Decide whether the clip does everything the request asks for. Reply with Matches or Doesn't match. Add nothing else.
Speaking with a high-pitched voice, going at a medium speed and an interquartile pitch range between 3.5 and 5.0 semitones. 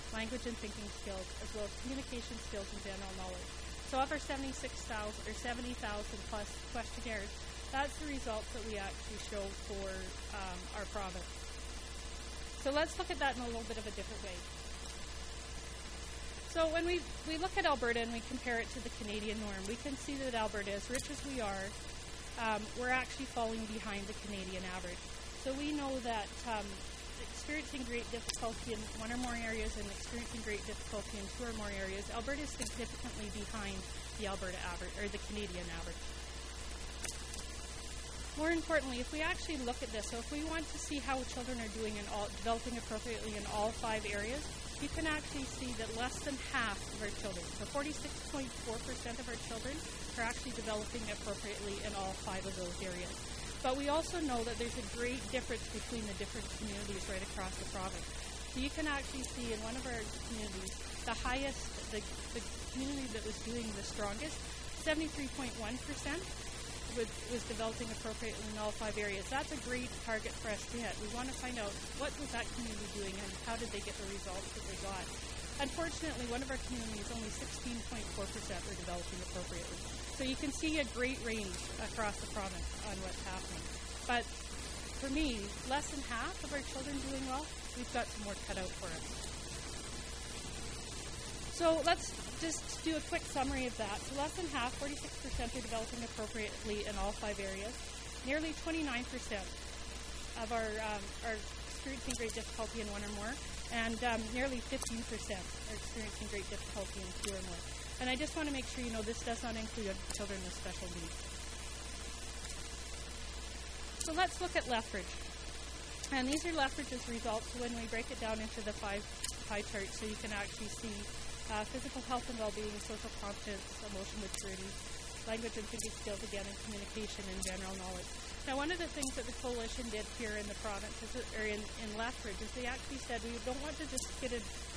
Matches